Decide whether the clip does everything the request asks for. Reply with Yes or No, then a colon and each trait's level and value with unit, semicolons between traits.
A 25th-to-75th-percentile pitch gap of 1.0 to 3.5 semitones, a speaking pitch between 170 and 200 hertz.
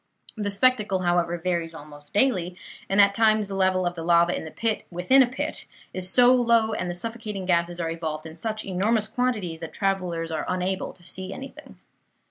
No: average, 4.0 semitones; medium, 185 Hz